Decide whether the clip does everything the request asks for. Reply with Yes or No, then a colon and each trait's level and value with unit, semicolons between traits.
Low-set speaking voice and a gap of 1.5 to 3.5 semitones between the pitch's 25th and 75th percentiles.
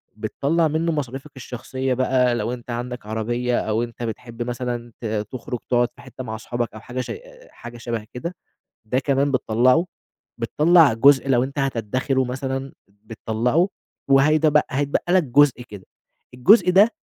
Yes: low, 125 Hz; average, 3.1 semitones